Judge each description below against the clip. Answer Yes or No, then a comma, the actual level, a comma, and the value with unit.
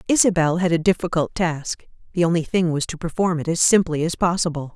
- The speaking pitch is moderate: Yes, medium, 170 Hz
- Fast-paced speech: No, average, 190 wpm